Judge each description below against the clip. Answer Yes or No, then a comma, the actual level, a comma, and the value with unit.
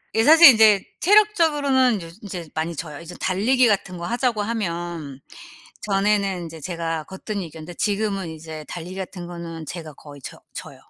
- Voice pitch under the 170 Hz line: No, medium, 185 Hz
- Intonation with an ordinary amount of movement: Yes, average, 4.8 semitones